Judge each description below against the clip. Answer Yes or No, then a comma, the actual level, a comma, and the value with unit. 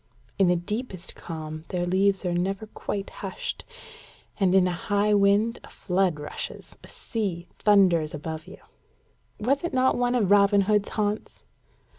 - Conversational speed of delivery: Yes, average, 155 wpm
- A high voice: Yes, high, 195 Hz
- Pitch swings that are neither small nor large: Yes, average, 3.1 semitones